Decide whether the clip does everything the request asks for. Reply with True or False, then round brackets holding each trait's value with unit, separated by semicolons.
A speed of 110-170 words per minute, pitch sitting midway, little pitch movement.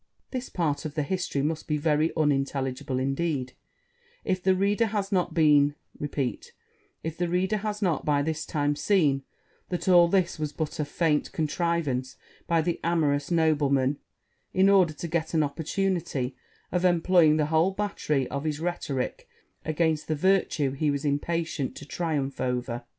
False (140 wpm; 155 Hz; 3.4 semitones)